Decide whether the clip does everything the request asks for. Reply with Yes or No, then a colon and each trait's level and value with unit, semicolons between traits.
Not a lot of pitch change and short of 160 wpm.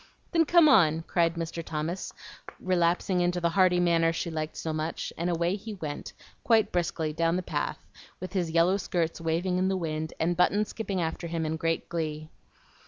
No: narrow, 2.3 semitones; average, 185 wpm